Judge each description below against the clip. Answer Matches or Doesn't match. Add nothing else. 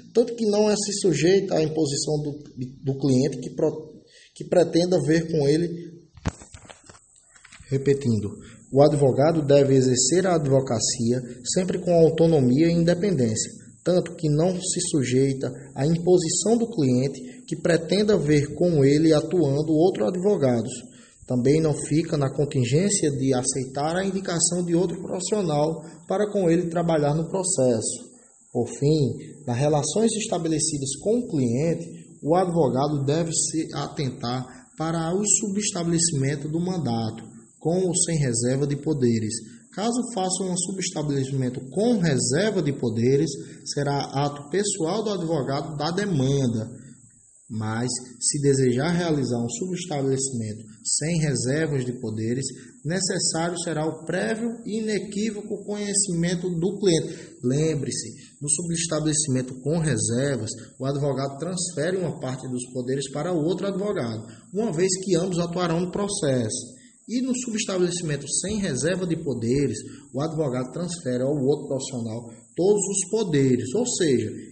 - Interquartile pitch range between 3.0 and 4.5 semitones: Doesn't match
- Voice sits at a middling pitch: Matches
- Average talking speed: Doesn't match